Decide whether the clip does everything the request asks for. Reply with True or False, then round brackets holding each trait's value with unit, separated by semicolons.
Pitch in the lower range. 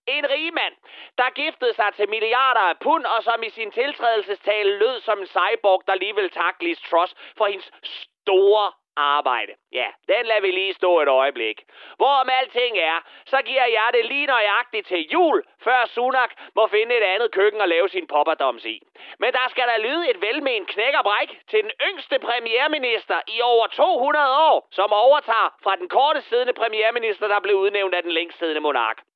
False (245 Hz)